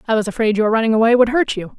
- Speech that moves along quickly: Yes, fast, 305 wpm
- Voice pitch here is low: No, high, 225 Hz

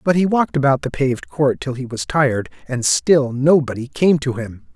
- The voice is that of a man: Yes, male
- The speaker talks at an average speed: No, fast, 215 wpm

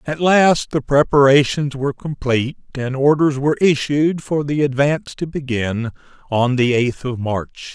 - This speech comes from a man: Yes, male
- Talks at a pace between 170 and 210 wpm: No, average, 155 wpm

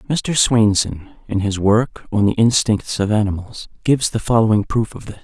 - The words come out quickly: No, average, 185 wpm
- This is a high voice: No, low, 110 Hz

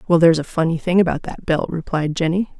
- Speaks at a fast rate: Yes, fast, 230 wpm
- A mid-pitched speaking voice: Yes, medium, 170 Hz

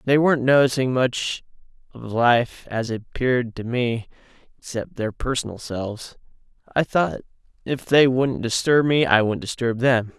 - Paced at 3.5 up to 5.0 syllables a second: Yes, 4.7 syllables/s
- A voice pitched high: No, low, 125 Hz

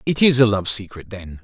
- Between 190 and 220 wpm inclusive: No, fast, 250 wpm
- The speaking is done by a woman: No, male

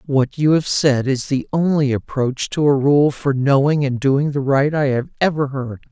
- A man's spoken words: Yes, male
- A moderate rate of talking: No, fast, 215 wpm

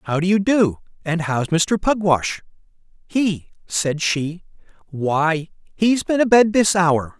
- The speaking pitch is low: No, medium, 180 Hz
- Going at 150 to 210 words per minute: No, average, 140 wpm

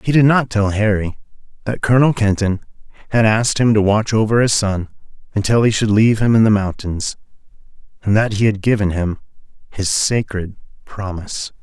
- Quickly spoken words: No, average, 170 wpm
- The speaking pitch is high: No, low, 105 Hz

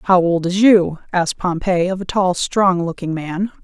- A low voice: No, medium, 180 Hz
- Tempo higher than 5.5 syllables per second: No, 4.4 syllables/s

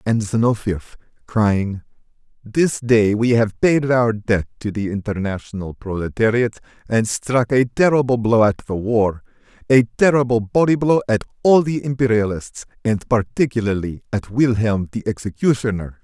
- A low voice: Yes, low, 115 Hz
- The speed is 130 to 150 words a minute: Yes, slow, 135 wpm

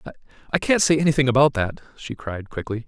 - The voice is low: Yes, low, 130 Hz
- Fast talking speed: No, average, 190 wpm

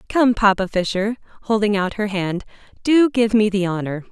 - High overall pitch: Yes, high, 210 Hz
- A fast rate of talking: No, average, 175 wpm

